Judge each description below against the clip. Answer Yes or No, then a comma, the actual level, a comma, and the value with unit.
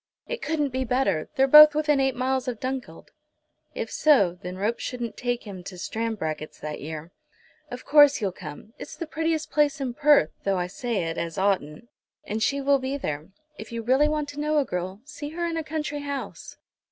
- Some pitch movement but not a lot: No, wide, 7.3 semitones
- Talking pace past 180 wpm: Yes, average, 200 wpm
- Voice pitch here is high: Yes, very high, 255 Hz